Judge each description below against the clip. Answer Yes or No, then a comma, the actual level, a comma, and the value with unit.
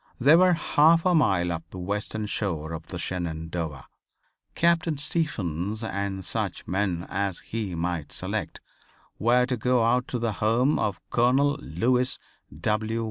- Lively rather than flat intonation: Yes, wide, 6.2 semitones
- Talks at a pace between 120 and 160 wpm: Yes, average, 150 wpm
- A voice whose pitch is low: Yes, low, 105 Hz